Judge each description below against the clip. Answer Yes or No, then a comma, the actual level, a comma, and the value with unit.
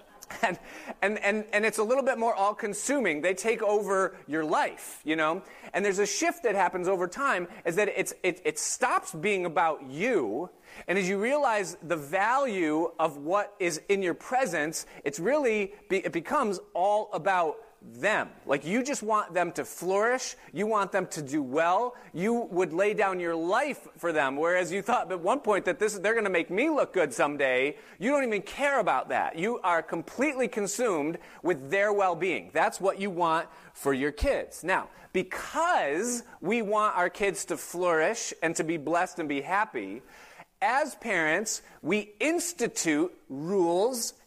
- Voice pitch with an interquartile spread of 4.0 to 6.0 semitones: Yes, average, 4.3 semitones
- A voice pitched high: Yes, high, 195 Hz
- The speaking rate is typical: Yes, average, 180 wpm